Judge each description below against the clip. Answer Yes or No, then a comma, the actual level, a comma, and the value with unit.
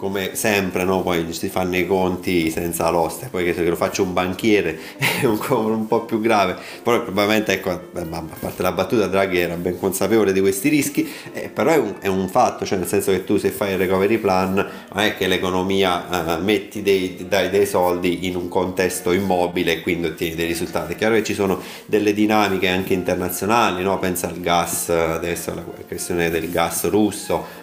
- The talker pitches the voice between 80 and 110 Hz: Yes, very low, 95 Hz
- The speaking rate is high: Yes, fast, 205 wpm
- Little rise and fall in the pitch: Yes, narrow, 1.8 semitones